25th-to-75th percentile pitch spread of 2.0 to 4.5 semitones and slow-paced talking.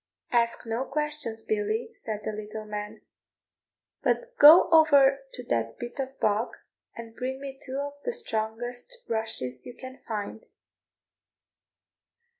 Yes: average, 4.2 semitones; slow, 130 wpm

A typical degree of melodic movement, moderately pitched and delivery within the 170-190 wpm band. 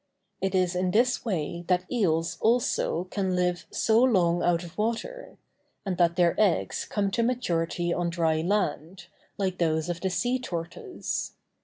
No: average, 3.7 semitones; medium, 180 Hz; average, 160 wpm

